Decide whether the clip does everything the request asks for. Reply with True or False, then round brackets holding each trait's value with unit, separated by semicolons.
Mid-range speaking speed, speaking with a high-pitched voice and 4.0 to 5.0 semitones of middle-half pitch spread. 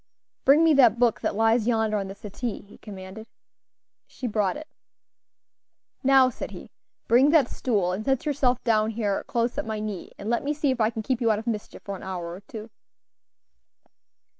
False (195 wpm; 225 Hz; 3.5 semitones)